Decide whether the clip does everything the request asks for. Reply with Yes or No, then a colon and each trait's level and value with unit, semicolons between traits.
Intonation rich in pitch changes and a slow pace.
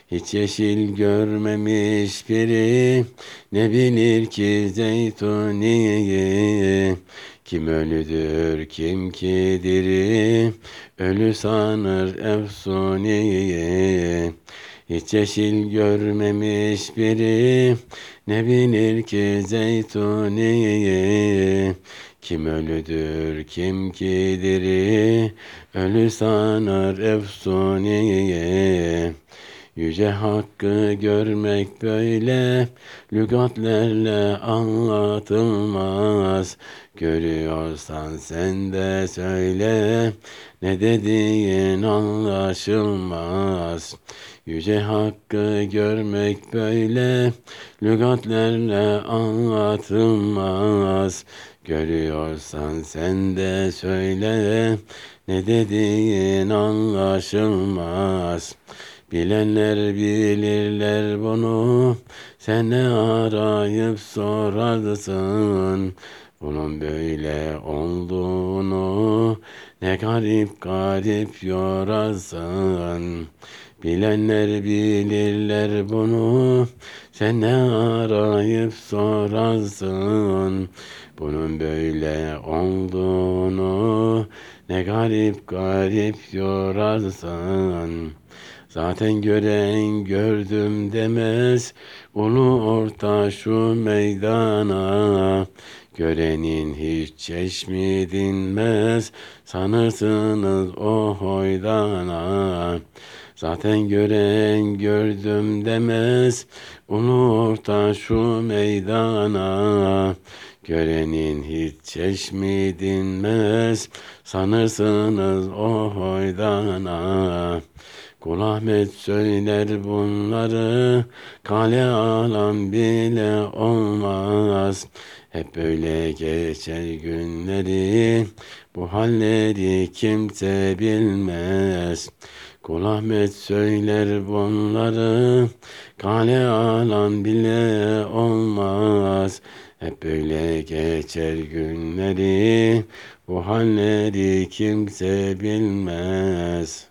No: narrow, 2.5 semitones; slow, 60 wpm